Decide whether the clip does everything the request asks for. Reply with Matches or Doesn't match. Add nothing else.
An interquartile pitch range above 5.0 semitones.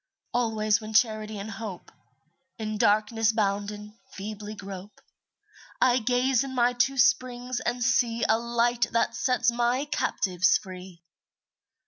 Doesn't match